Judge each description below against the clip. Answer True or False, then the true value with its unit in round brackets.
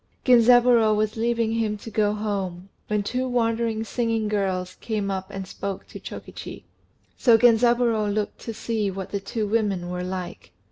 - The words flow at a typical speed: True (160 wpm)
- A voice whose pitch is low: False (215 Hz)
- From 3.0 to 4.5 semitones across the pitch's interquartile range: False (2.6 semitones)